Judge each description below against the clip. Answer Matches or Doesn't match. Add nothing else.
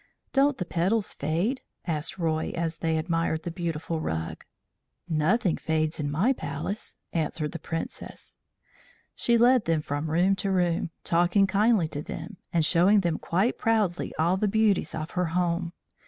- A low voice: Doesn't match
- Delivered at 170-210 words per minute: Doesn't match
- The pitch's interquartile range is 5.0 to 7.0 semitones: Doesn't match